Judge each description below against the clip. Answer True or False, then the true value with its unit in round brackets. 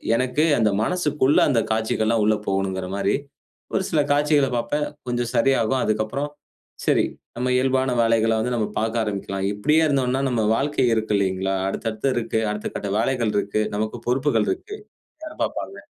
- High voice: False (115 Hz)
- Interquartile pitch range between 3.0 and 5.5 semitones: True (4.0 semitones)